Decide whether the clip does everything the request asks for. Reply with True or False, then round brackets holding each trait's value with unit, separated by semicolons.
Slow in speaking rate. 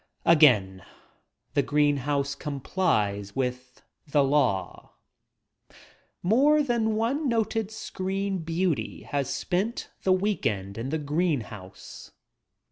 True (110 wpm)